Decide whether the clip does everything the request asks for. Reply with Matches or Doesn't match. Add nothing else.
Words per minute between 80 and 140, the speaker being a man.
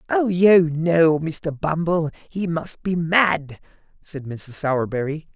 Matches